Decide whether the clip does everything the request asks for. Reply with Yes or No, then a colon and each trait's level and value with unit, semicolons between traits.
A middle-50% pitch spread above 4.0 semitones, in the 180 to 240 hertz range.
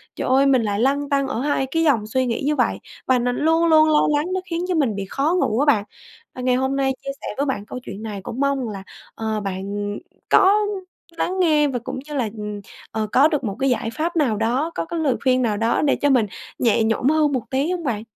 No: average, 4.9 semitones; very high, 265 Hz